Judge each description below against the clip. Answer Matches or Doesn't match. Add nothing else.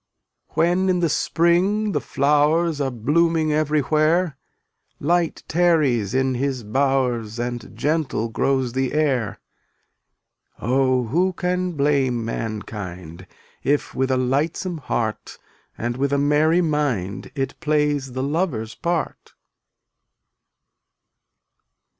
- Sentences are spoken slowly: Matches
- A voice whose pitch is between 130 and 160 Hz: Matches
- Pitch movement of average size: Matches